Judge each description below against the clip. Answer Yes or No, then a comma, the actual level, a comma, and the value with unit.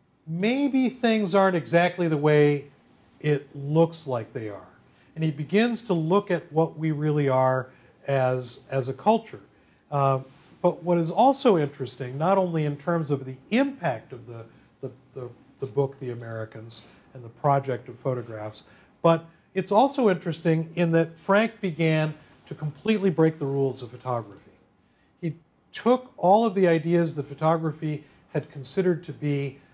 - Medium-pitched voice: Yes, medium, 150 Hz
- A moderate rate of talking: Yes, average, 155 wpm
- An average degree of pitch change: Yes, average, 4.7 semitones